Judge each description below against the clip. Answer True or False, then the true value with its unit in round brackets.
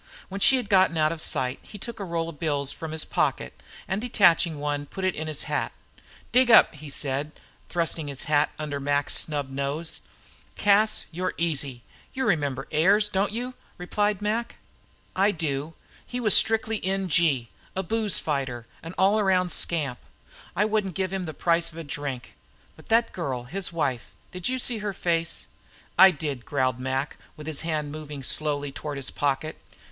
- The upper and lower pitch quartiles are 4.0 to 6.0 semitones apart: True (5.1 semitones)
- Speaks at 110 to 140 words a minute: False (180 wpm)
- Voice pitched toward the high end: False (165 Hz)